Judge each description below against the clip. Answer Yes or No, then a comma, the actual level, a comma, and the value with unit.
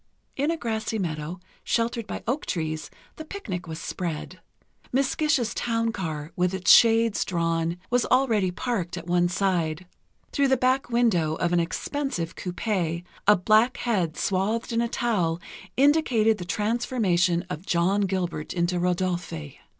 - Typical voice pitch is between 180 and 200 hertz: Yes, high, 190 Hz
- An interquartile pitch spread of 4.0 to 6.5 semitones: Yes, average, 5.2 semitones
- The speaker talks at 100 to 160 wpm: Yes, average, 150 wpm